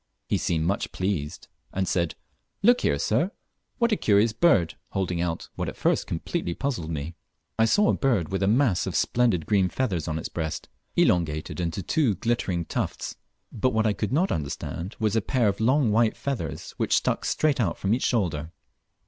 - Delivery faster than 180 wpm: Yes, average, 190 wpm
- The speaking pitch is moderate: No, low, 100 Hz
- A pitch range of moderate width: No, wide, 5.9 semitones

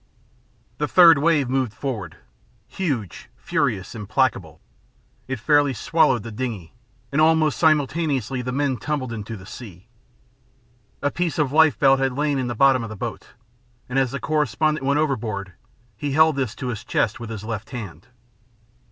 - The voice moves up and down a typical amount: Yes, average, 4.6 semitones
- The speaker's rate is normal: Yes, average, 160 wpm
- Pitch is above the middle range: No, low, 130 Hz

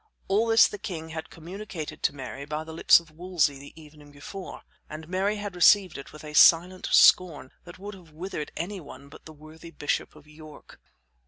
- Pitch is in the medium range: Yes, medium, 160 Hz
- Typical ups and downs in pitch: Yes, average, 3.5 semitones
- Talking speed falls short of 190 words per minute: No, average, 195 wpm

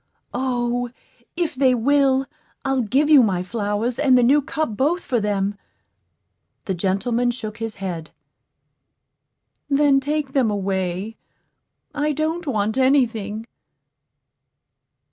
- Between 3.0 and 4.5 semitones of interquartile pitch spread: No, average, 4.9 semitones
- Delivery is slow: Yes, slow, 120 wpm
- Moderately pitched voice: No, high, 245 Hz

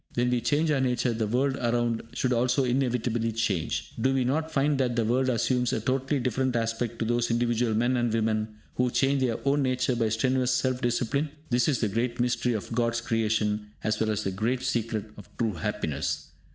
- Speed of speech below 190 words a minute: No, fast, 205 wpm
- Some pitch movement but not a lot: No, narrow, 2.3 semitones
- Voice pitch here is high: No, low, 120 Hz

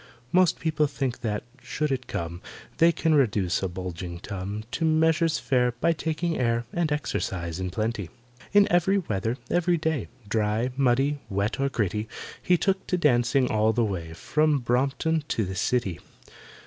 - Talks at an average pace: Yes, average, 160 wpm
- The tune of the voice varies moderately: No, wide, 7.4 semitones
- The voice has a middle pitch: No, low, 125 Hz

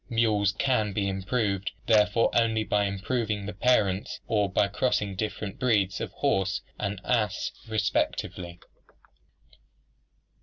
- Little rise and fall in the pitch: Yes, narrow, 2.1 semitones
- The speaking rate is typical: No, slow, 120 wpm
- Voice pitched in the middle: No, low, 105 Hz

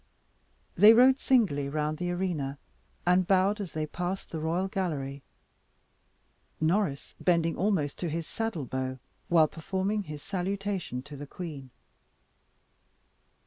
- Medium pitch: Yes, medium, 175 Hz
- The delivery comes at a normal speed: No, slow, 125 wpm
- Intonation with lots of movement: No, average, 4.4 semitones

